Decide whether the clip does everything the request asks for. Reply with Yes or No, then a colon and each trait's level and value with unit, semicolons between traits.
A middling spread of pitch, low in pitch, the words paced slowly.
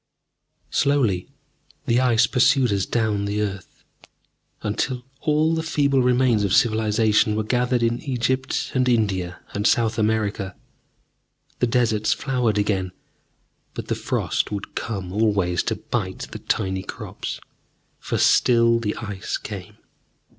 Yes: average, 3.4 semitones; low, 110 Hz; slow, 130 wpm